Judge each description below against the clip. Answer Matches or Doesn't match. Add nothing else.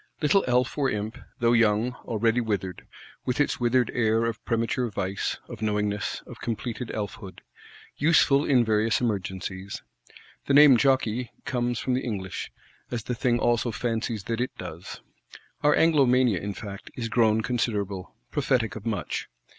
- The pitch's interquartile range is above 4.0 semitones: Doesn't match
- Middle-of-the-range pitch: Doesn't match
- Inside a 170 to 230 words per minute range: Doesn't match